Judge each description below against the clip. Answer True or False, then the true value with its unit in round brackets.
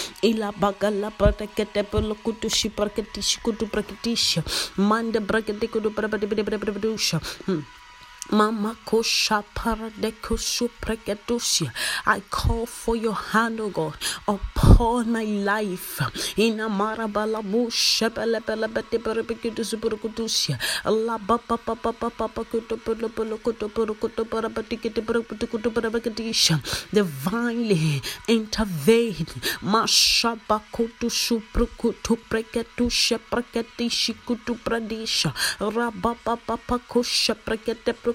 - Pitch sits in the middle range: False (225 Hz)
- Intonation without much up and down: True (1.4 semitones)